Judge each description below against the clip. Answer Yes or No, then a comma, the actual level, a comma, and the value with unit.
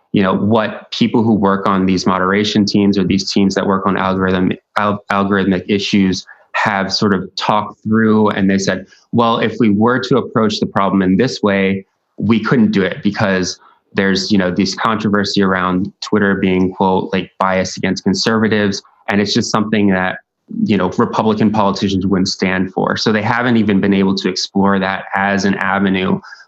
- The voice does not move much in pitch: Yes, narrow, 1.5 semitones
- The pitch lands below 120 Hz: Yes, low, 100 Hz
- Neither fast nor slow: Yes, average, 185 wpm